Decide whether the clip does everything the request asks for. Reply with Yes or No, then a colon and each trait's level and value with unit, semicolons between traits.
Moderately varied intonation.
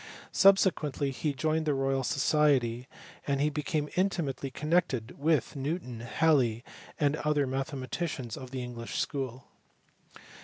Yes: average, 3.1 semitones